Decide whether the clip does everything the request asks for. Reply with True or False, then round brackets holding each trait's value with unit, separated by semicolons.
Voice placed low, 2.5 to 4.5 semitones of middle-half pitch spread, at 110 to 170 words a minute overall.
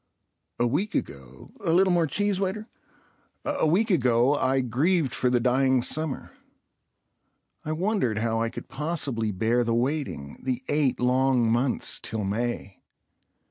False (130 Hz; 5.2 semitones; 140 wpm)